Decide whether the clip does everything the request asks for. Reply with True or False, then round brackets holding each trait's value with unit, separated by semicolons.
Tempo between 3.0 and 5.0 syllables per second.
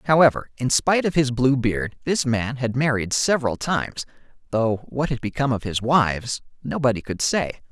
False (5.3 syllables/s)